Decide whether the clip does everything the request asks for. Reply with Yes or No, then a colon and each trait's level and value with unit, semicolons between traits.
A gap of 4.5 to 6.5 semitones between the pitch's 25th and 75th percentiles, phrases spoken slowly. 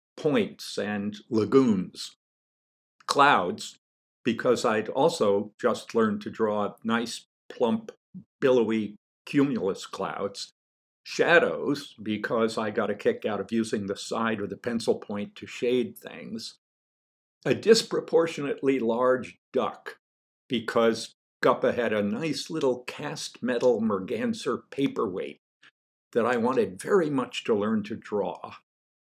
Yes: wide, 5.5 semitones; slow, 120 wpm